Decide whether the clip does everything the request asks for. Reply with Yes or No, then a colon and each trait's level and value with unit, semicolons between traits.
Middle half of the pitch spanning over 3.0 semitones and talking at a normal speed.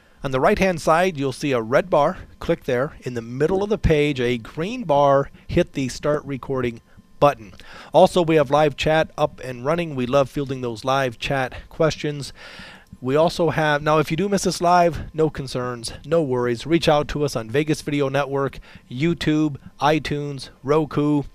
Yes: average, 3.4 semitones; average, 185 wpm